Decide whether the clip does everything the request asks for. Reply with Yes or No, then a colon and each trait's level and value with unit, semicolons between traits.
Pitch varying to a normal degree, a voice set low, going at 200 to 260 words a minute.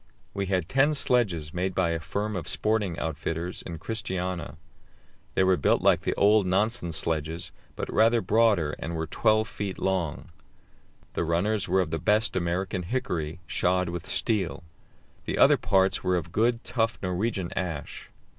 No: average, 4.1 semitones; very low, 95 Hz; average, 160 wpm